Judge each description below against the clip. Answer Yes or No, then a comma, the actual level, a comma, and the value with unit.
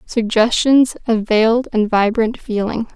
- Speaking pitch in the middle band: No, high, 225 Hz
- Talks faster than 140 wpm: No, slow, 120 wpm